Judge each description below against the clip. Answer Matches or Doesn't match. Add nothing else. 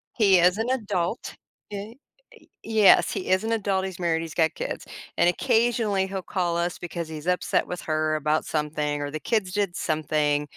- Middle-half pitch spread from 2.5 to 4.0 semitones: Doesn't match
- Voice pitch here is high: Doesn't match